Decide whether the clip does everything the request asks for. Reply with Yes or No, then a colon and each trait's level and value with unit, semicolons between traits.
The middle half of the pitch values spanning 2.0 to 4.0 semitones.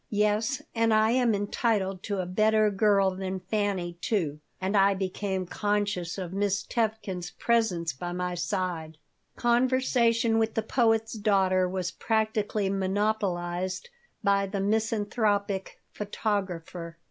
Yes: average, 2.9 semitones